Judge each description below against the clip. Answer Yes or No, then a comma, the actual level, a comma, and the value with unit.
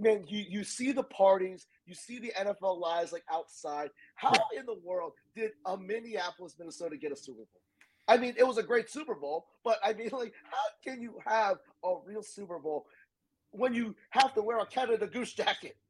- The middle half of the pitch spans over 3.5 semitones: Yes, wide, 5.4 semitones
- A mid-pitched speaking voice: No, high, 210 Hz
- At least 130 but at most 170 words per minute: No, fast, 205 wpm